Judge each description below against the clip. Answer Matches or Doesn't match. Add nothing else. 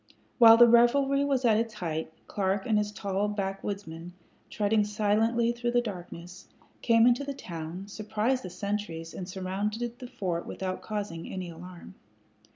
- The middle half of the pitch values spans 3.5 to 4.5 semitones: Matches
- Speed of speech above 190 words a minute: Doesn't match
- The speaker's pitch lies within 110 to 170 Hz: Doesn't match